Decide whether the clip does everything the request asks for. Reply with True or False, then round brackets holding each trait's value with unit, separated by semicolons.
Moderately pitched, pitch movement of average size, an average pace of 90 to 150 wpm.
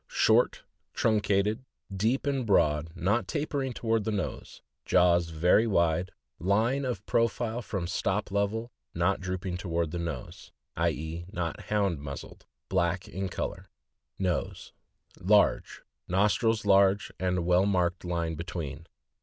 False (95 Hz; 3.8 semitones; 140 wpm)